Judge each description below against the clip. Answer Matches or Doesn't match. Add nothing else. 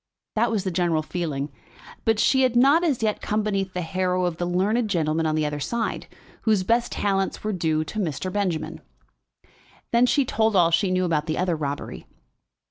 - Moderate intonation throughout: Matches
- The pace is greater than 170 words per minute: Matches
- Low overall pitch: Doesn't match